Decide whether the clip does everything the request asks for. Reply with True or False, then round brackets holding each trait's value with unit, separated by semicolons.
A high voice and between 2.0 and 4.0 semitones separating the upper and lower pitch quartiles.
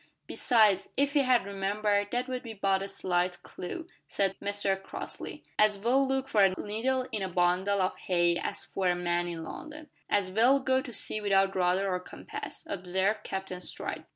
False (200 Hz; 4.4 semitones)